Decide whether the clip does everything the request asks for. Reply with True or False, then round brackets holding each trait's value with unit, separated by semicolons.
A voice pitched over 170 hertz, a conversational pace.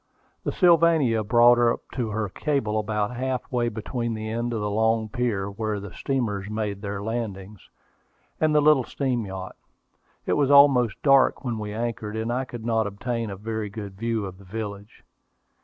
False (110 Hz; 180 wpm)